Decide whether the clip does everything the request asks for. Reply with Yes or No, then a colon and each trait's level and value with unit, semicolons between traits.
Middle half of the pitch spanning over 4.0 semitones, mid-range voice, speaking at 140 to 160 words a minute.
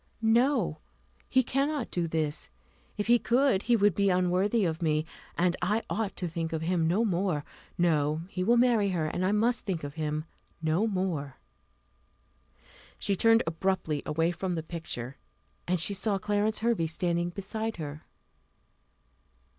Yes: average, 4.7 semitones; medium, 180 Hz; average, 155 wpm